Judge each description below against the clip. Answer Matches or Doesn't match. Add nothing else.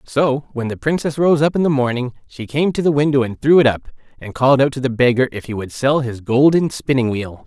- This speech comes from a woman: Doesn't match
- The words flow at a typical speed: Doesn't match